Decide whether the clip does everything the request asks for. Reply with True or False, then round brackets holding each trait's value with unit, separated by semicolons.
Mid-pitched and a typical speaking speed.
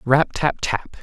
True (145 Hz; 175 wpm)